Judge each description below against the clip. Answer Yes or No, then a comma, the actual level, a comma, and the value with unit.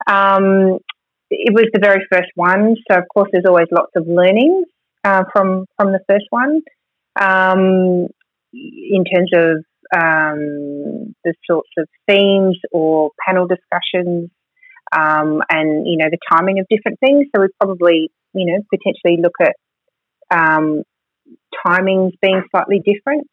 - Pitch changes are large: No, average, 2.9 semitones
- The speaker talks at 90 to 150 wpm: Yes, average, 140 wpm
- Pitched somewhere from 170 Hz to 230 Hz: Yes, high, 190 Hz